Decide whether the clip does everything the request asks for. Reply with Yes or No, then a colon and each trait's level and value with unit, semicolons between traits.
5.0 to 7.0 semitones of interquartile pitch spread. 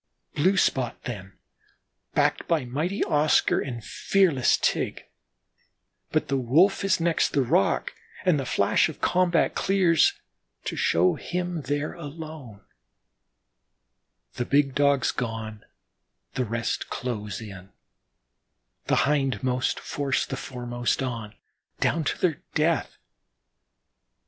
Yes: average, 5.3 semitones